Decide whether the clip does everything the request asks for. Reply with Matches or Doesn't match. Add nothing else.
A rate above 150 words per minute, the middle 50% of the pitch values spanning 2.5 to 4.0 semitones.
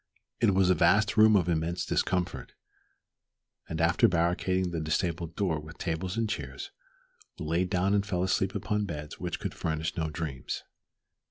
Matches